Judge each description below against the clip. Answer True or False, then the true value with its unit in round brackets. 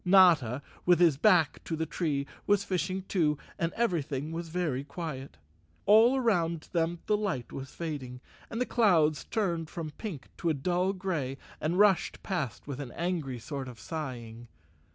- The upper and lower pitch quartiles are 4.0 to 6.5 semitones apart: True (4.8 semitones)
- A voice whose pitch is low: False (165 Hz)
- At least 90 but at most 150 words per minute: False (165 wpm)